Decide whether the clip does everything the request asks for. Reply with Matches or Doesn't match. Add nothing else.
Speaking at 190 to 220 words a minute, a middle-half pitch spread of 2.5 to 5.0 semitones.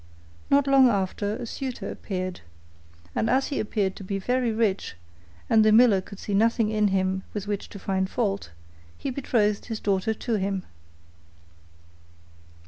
Doesn't match